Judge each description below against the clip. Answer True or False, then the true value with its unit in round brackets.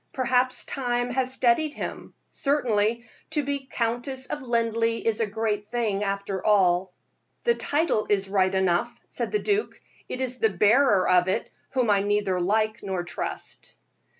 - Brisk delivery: False (155 wpm)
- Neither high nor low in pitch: False (225 Hz)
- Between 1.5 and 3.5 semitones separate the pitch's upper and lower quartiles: False (4.4 semitones)